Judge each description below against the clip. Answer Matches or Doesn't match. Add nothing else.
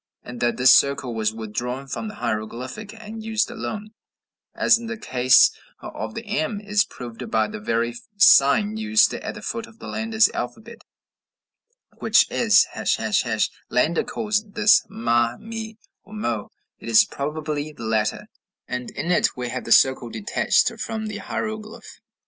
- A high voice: Doesn't match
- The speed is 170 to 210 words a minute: Doesn't match